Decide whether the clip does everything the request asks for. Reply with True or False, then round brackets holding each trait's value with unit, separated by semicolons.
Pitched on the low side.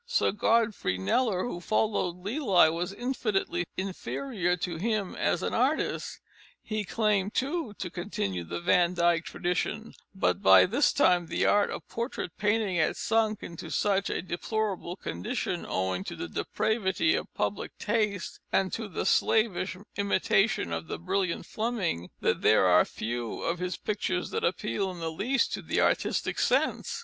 False (190 Hz)